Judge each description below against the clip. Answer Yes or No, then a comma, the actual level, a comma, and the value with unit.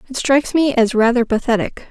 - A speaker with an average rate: Yes, average, 190 wpm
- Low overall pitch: No, very high, 250 Hz